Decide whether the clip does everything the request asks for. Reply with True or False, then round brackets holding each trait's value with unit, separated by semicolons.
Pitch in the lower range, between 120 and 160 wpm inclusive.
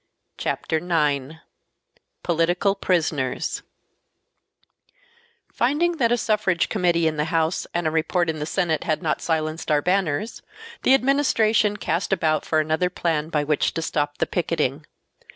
False (165 Hz; 140 wpm)